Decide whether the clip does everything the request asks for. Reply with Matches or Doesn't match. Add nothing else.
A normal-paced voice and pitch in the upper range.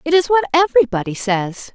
Matches